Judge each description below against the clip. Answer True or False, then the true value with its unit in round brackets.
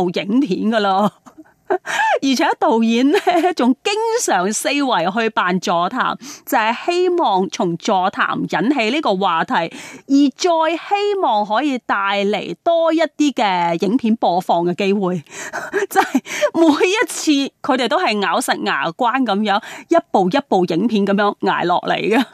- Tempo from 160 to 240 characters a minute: True (215 characters per minute)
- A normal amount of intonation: False (8.6 semitones)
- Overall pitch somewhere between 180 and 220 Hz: False (265 Hz)